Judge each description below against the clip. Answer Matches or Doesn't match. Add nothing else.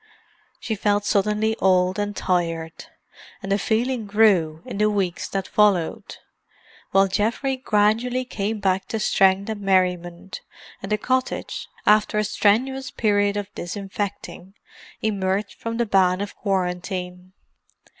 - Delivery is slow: Matches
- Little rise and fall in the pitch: Matches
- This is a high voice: Matches